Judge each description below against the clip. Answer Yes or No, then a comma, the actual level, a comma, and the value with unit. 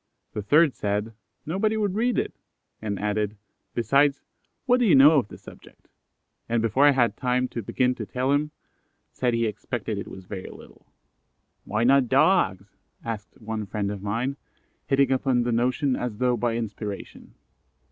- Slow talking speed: No, average, 165 wpm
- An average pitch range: Yes, average, 4.5 semitones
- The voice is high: No, low, 120 Hz